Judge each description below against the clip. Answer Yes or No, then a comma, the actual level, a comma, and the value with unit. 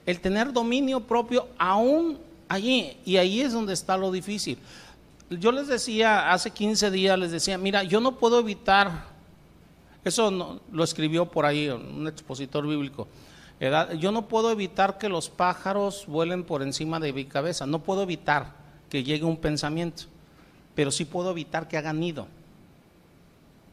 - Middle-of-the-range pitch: Yes, medium, 180 Hz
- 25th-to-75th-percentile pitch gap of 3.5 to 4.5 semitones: No, average, 5.1 semitones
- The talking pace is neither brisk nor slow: Yes, average, 160 wpm